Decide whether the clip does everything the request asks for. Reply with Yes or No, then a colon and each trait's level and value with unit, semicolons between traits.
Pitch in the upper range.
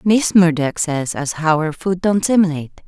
No: medium, 170 Hz